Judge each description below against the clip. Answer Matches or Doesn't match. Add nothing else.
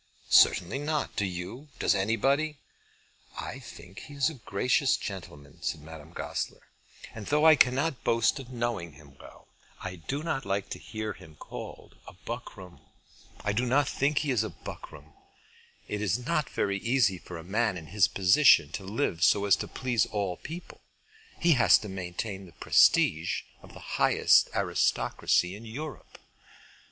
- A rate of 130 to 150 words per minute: Doesn't match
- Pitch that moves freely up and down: Matches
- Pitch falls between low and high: Doesn't match